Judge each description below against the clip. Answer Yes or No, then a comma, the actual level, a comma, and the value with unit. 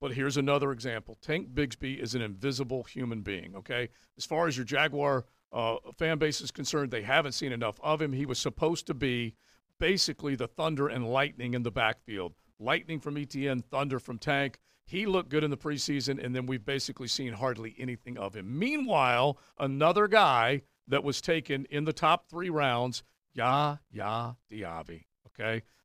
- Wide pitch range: No, average, 3.4 semitones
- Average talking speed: Yes, average, 175 wpm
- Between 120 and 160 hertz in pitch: Yes, low, 135 Hz